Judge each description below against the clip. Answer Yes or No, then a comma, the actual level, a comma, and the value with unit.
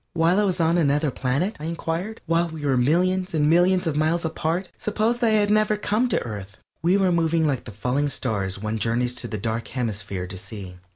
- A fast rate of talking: Yes, fast, 220 wpm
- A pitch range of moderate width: No, wide, 7.1 semitones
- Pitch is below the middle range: No, medium, 160 Hz